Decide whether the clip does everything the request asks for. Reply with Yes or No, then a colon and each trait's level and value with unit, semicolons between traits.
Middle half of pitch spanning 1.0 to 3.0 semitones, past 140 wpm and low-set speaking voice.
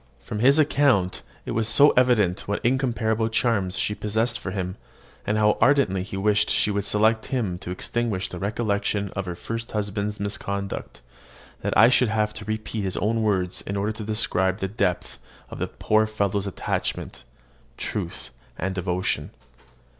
Yes: narrow, 2.5 semitones; average, 165 wpm; low, 105 Hz